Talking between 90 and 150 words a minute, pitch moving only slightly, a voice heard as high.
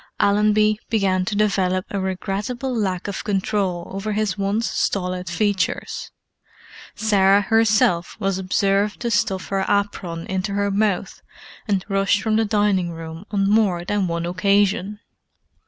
Yes: average, 140 wpm; narrow, 2.0 semitones; high, 200 Hz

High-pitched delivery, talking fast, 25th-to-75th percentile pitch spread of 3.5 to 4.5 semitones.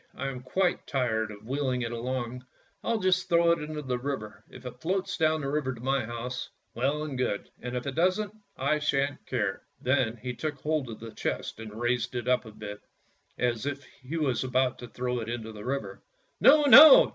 No: low, 130 Hz; fast, 215 wpm; average, 3.9 semitones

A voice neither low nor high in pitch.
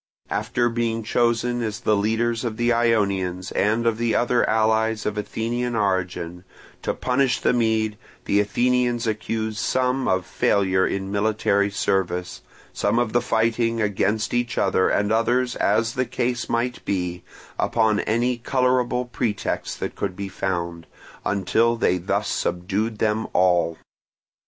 No: low, 110 Hz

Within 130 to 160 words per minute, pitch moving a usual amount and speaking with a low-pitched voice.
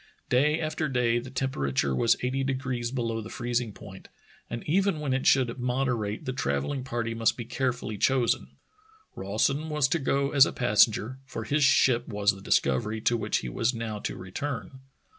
No: average, 185 wpm; average, 3.3 semitones; low, 125 Hz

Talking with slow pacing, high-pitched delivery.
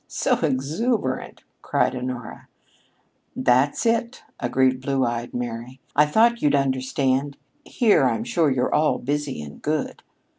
No: slow, 125 wpm; low, 135 Hz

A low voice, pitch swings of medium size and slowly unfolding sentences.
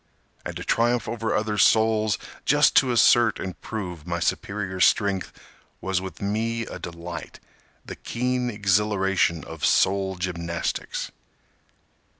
Yes: low, 100 Hz; average, 3.7 semitones; slow, 125 wpm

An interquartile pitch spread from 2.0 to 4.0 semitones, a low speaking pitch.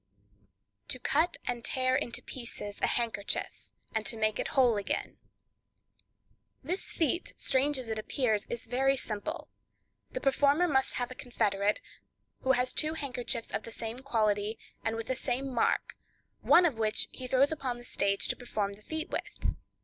No: average, 3.6 semitones; high, 245 Hz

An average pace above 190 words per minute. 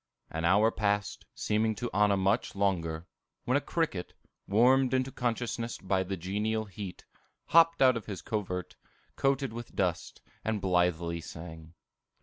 No: average, 140 wpm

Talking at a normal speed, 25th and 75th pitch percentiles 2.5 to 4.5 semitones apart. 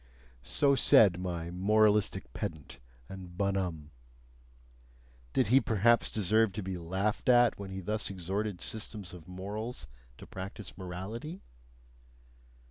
No: slow, 120 wpm; average, 3.2 semitones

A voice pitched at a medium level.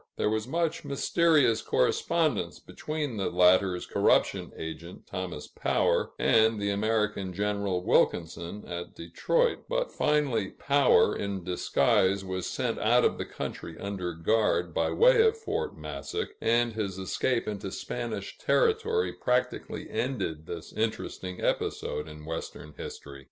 No: low, 105 Hz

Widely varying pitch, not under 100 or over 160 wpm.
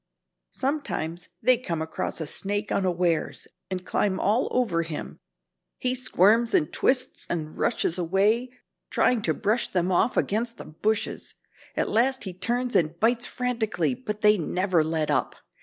Yes: wide, 5.8 semitones; average, 150 wpm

